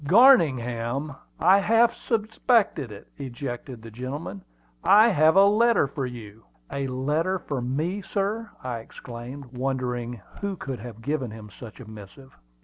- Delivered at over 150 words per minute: No, average, 145 wpm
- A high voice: No, low, 135 Hz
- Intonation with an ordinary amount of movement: No, wide, 8.0 semitones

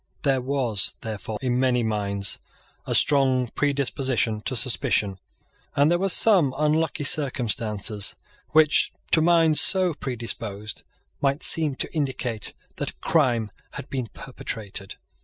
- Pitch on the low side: Yes, low, 130 Hz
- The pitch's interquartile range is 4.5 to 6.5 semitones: Yes, average, 5.2 semitones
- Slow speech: Yes, slow, 125 wpm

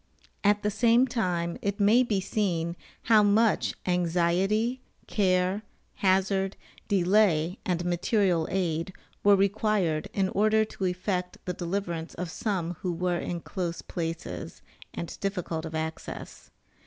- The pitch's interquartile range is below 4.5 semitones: Yes, average, 3.1 semitones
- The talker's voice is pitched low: No, medium, 185 Hz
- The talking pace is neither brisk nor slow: No, slow, 130 wpm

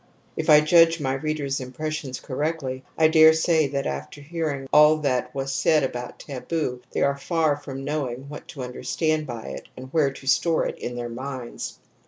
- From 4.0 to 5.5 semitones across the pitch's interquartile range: No, average, 3.2 semitones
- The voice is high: No, medium, 140 Hz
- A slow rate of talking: No, average, 185 wpm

